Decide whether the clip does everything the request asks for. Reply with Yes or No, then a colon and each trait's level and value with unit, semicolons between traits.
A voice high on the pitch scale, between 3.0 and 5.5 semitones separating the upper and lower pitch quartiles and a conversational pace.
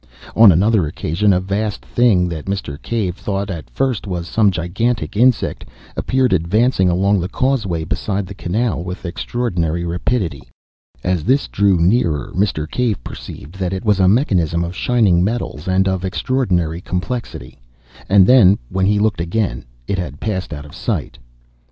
No: very low, 95 Hz; average, 4.0 semitones; average, 160 wpm